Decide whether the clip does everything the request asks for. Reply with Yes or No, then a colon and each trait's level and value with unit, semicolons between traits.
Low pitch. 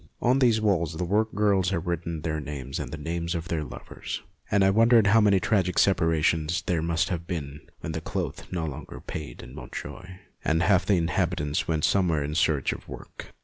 Yes: very low, 85 Hz